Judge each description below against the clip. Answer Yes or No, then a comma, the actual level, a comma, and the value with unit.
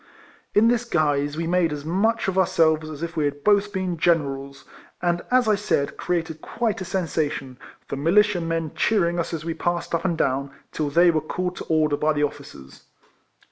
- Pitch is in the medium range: Yes, medium, 165 Hz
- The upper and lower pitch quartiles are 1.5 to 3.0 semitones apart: No, average, 3.7 semitones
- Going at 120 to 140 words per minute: No, average, 200 wpm